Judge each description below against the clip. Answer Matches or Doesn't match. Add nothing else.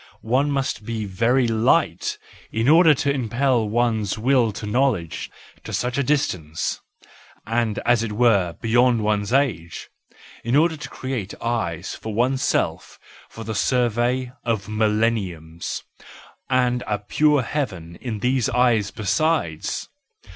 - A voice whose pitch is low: Matches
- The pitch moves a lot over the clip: Doesn't match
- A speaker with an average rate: Doesn't match